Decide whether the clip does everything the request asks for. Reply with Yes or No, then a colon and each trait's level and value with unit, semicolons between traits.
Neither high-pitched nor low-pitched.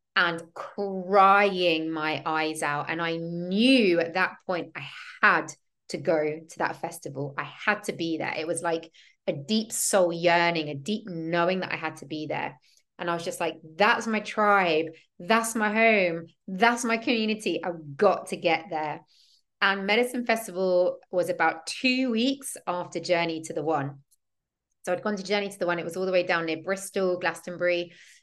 Yes: medium, 175 Hz